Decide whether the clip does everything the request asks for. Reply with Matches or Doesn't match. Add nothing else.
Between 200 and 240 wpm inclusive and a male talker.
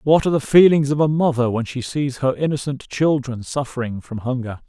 Matches